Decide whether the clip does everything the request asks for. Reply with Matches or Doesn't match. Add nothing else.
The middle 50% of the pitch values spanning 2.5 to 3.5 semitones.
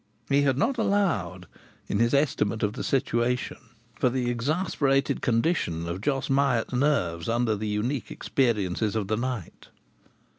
Doesn't match